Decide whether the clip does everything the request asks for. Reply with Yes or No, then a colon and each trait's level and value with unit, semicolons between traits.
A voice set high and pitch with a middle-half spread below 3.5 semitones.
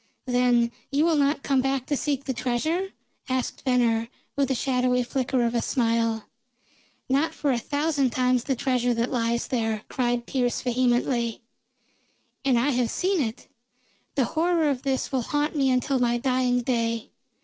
Yes: very high, 255 Hz; narrow, 2.5 semitones